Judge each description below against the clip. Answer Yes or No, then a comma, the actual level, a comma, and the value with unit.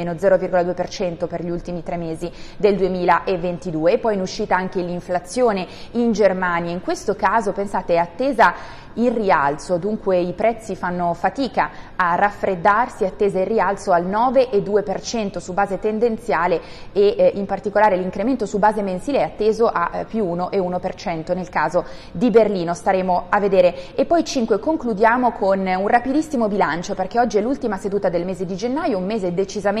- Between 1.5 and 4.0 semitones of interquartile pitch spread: Yes, average, 3.6 semitones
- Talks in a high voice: Yes, high, 195 Hz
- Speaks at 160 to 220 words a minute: Yes, average, 165 wpm